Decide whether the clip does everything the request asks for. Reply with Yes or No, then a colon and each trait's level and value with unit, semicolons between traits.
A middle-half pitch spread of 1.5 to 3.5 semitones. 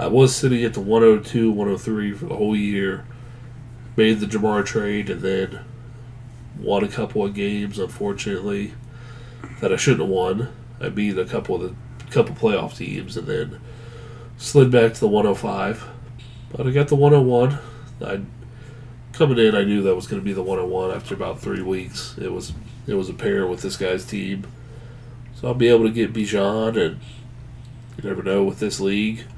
Yes: average, 3.0 semitones